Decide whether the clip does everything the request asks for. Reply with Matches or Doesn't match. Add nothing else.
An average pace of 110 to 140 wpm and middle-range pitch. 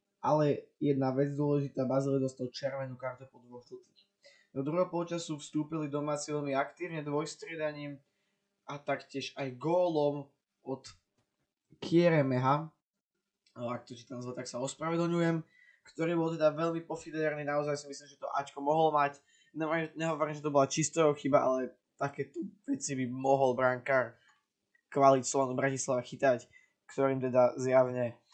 Matches